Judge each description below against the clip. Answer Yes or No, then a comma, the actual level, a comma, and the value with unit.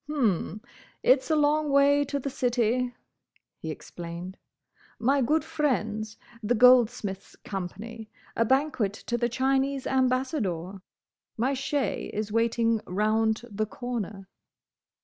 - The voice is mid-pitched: No, high, 240 Hz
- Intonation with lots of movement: No, average, 4.0 semitones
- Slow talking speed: Yes, slow, 110 wpm